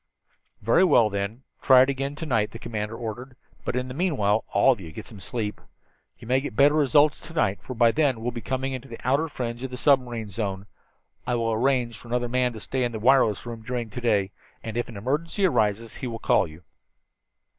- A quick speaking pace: Yes, fast, 230 wpm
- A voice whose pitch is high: No, low, 120 Hz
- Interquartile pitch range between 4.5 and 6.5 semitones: No, average, 3.1 semitones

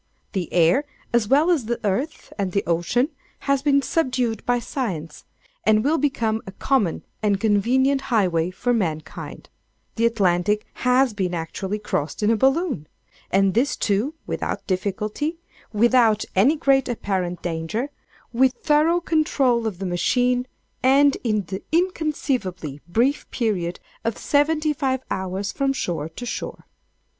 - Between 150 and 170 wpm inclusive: No, slow, 135 wpm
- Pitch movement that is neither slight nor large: No, wide, 6.1 semitones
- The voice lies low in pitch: No, high, 230 Hz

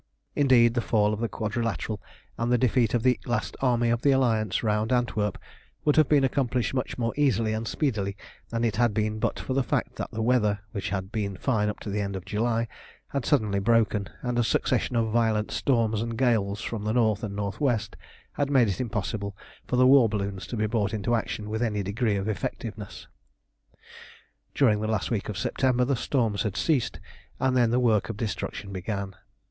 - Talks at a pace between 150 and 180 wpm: No, fast, 205 wpm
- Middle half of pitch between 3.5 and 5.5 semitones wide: No, average, 2.7 semitones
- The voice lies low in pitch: Yes, low, 115 Hz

